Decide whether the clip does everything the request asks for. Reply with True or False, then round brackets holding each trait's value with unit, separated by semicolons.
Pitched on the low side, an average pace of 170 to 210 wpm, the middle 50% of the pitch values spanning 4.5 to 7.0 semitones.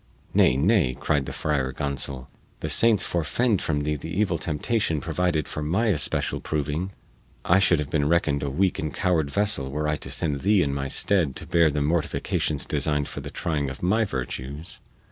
False (75 Hz; 190 wpm; 4.0 semitones)